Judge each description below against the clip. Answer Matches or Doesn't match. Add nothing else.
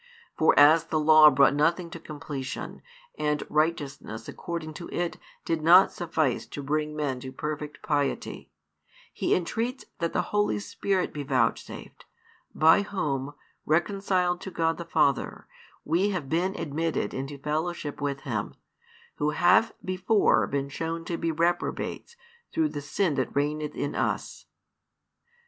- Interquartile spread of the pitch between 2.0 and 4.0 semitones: Matches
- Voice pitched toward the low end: Doesn't match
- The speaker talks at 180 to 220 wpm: Doesn't match